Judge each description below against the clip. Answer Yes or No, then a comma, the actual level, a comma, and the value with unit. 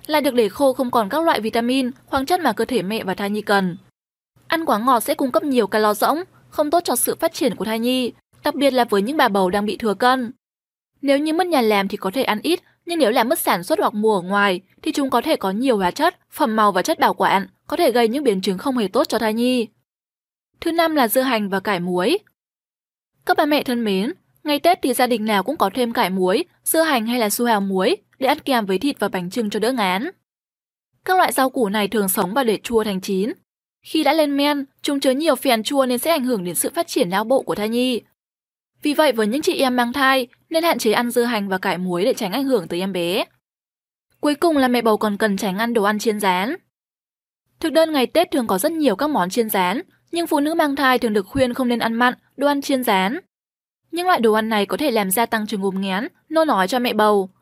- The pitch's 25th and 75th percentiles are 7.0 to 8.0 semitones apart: No, wide, 5.5 semitones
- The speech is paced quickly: Yes, fast, 265 wpm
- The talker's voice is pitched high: Yes, high, 245 Hz